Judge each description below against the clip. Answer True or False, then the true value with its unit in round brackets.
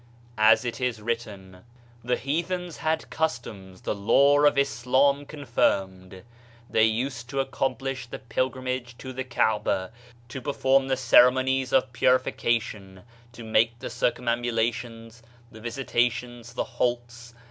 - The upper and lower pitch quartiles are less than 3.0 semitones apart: True (2.6 semitones)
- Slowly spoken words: True (130 wpm)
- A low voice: True (120 Hz)